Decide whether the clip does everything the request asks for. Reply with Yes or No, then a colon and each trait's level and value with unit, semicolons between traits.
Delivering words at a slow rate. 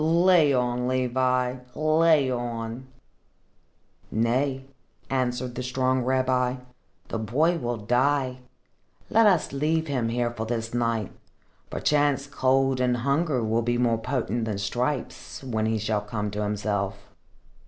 Yes: slow, 130 wpm